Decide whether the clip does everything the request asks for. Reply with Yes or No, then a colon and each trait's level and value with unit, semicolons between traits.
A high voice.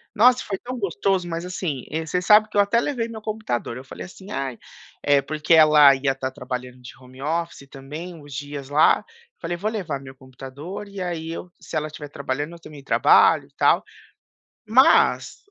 No: medium, 155 Hz